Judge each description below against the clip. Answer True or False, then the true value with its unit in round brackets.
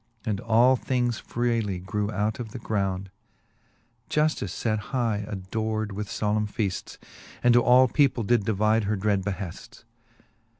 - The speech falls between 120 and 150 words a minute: True (140 wpm)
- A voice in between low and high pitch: False (110 Hz)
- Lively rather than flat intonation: False (2.7 semitones)